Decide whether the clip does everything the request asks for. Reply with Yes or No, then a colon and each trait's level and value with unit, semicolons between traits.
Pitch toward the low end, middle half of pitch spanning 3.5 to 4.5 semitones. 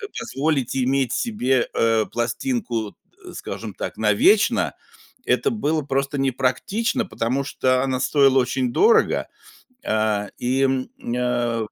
No: low, 130 Hz; average, 3.0 semitones